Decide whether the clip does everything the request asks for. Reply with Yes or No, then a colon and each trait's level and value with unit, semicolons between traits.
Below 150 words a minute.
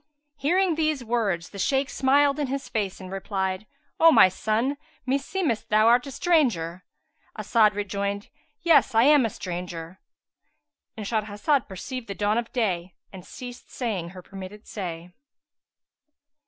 Yes: average, 140 wpm